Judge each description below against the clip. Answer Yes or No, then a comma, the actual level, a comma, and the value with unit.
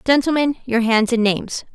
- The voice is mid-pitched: No, high, 245 Hz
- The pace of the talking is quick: No, average, 170 wpm